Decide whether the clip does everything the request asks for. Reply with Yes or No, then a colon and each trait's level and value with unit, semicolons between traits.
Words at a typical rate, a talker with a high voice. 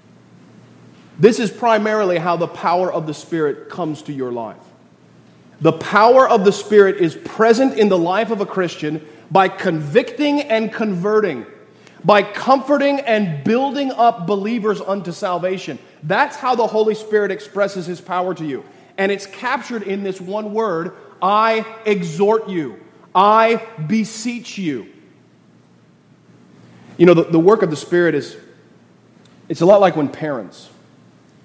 Yes: average, 145 wpm; high, 200 Hz